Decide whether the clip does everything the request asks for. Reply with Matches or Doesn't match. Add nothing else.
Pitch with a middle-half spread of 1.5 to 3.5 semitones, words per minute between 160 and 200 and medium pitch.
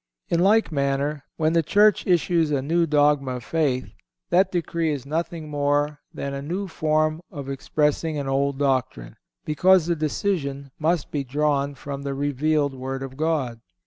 Matches